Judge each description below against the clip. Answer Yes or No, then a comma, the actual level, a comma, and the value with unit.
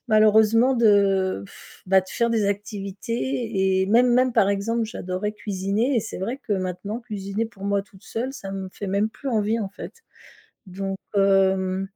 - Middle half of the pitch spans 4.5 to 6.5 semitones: No, average, 2.8 semitones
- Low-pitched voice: No, high, 205 Hz